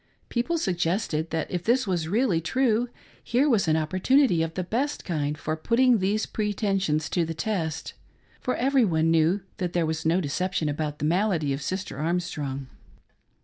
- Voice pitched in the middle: Yes, medium, 180 Hz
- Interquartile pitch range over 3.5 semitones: Yes, wide, 5.4 semitones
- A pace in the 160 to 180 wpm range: Yes, average, 170 wpm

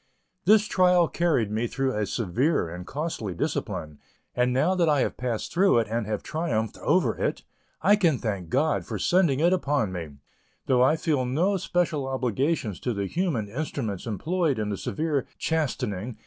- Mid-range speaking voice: No, low, 130 Hz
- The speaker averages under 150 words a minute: No, average, 175 wpm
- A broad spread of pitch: Yes, wide, 7.2 semitones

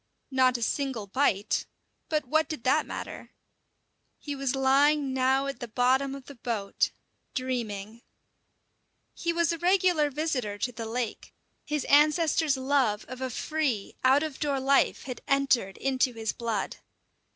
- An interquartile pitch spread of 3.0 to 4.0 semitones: Yes, average, 3.3 semitones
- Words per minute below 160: Yes, average, 150 wpm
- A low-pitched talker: No, very high, 265 Hz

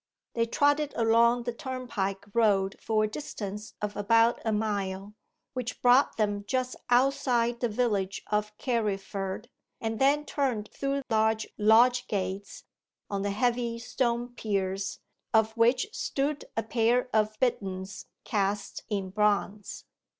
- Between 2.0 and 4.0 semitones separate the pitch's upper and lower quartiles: Yes, average, 3.1 semitones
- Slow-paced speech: Yes, slow, 130 wpm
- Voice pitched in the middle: No, high, 220 Hz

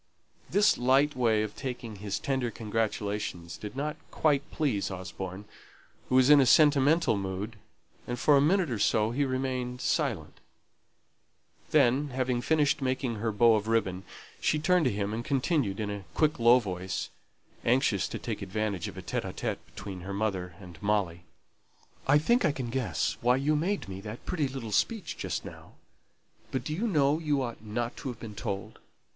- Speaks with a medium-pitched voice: No, low, 120 Hz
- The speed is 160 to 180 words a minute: Yes, average, 175 wpm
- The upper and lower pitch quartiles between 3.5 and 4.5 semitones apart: No, average, 5.3 semitones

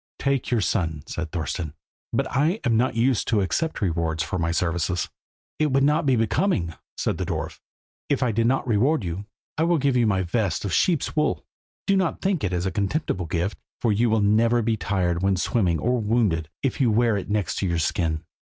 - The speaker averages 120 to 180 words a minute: No, fast, 205 wpm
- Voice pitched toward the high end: No, low, 105 Hz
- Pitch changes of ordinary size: No, wide, 6.3 semitones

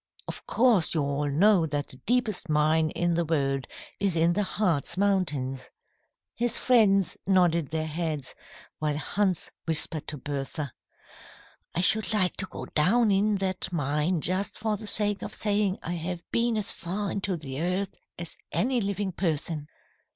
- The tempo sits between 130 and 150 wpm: No, average, 160 wpm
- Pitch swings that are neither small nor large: Yes, average, 4.8 semitones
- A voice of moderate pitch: Yes, medium, 175 Hz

